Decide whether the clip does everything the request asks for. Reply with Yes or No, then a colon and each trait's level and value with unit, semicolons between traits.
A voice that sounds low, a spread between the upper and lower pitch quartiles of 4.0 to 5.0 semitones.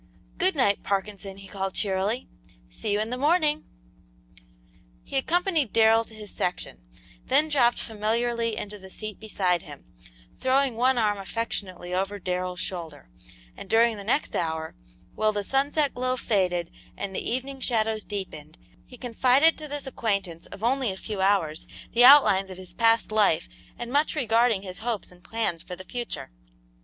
No: high, 215 Hz; average, 4.6 semitones